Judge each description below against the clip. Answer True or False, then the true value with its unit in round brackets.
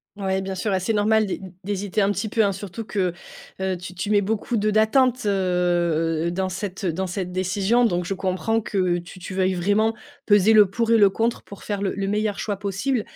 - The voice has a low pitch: False (195 Hz)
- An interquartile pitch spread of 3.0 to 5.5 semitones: False (2.5 semitones)